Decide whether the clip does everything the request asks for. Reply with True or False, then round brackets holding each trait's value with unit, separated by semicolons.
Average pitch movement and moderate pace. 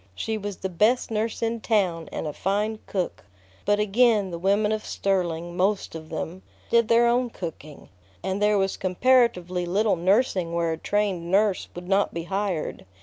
True (3.6 semitones; 175 wpm)